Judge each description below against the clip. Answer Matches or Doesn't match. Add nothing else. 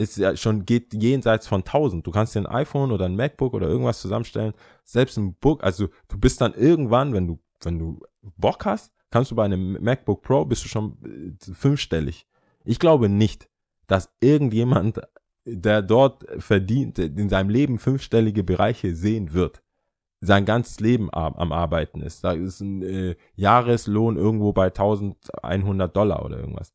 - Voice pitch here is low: Matches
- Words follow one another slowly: Doesn't match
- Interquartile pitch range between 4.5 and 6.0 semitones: Doesn't match